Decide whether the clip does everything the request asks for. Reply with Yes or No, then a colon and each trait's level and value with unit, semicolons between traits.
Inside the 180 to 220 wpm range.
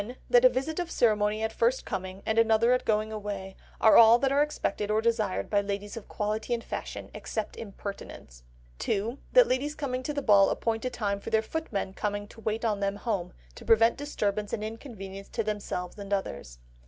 Yes: average, 195 wpm